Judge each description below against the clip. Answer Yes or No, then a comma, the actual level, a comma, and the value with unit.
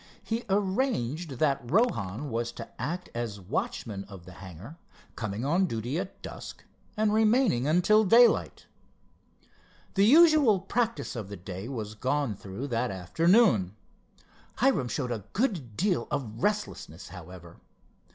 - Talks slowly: Yes, slow, 130 wpm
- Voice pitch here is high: No, low, 135 Hz